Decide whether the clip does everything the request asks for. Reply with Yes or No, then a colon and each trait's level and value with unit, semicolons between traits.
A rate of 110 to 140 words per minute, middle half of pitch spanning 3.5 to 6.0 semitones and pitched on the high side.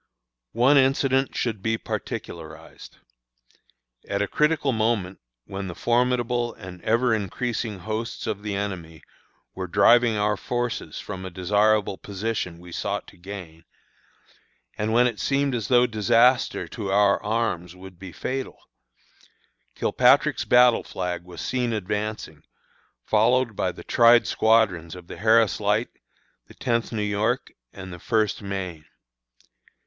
No: slow, 135 wpm; average, 4.0 semitones; low, 105 Hz